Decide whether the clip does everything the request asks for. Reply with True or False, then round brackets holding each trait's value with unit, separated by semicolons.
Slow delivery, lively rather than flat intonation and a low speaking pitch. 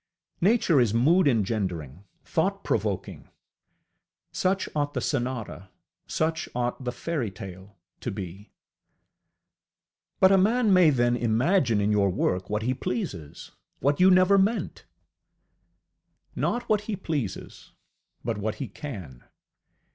True (120 wpm; 8.8 semitones; 120 Hz)